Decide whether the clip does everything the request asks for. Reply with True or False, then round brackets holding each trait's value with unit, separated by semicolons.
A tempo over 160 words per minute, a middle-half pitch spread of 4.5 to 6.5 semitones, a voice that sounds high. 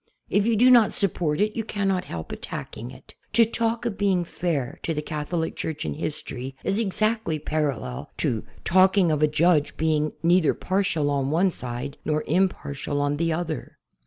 False (180 wpm; 5.0 semitones; 165 Hz)